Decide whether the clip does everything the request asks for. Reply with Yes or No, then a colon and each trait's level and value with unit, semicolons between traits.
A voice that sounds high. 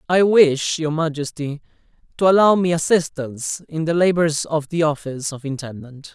No: medium, 155 Hz